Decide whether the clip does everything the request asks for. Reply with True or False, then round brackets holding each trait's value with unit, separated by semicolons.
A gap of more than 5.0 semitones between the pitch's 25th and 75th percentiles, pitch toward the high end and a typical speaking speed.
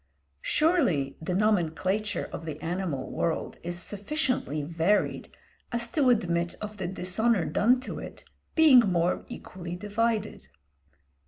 False (5.4 semitones; 195 Hz; 120 wpm)